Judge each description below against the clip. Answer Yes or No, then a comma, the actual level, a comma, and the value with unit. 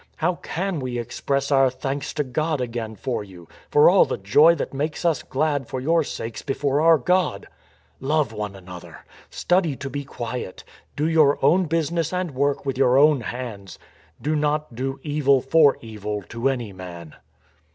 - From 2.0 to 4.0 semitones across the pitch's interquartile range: No, average, 4.5 semitones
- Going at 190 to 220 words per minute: No, average, 170 wpm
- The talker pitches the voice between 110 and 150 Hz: Yes, medium, 140 Hz